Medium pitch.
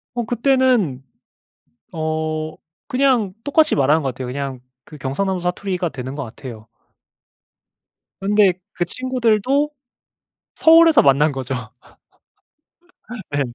Yes: medium, 175 Hz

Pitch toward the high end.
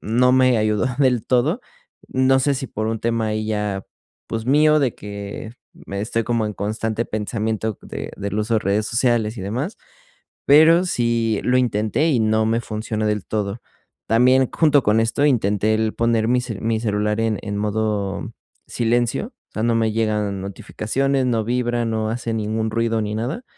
No: low, 115 Hz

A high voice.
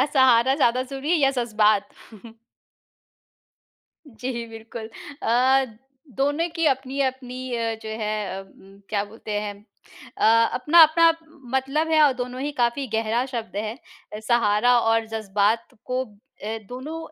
Yes: high, 245 Hz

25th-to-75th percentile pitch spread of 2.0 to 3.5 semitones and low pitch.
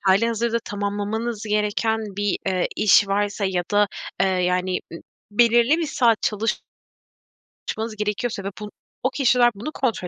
No: average, 2.8 semitones; high, 210 Hz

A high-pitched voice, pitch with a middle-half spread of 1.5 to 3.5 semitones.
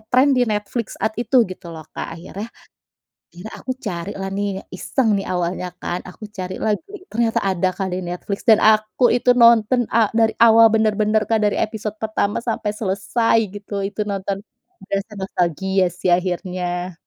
Yes: high, 205 Hz; average, 3.1 semitones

